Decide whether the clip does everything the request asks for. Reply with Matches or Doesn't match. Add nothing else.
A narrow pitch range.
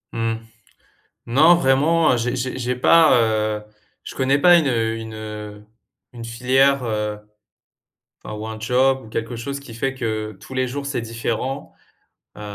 Doesn't match